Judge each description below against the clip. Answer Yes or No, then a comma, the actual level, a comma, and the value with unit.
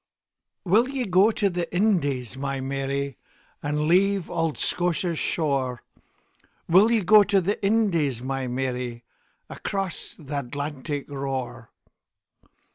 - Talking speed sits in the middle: No, slow, 105 wpm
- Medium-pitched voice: Yes, medium, 150 Hz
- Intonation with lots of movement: Yes, wide, 6.2 semitones